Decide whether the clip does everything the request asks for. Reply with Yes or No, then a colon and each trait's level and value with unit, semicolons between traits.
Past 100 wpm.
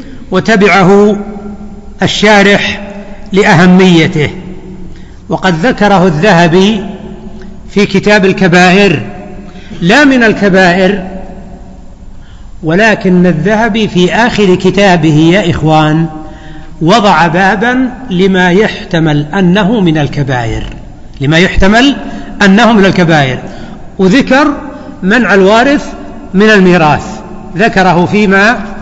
No: average, 80 wpm